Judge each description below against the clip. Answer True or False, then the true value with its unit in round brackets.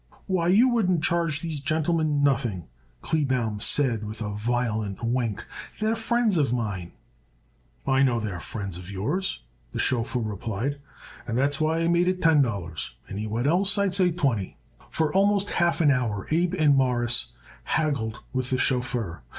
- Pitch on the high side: False (135 Hz)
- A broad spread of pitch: True (7.1 semitones)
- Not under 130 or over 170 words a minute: True (160 wpm)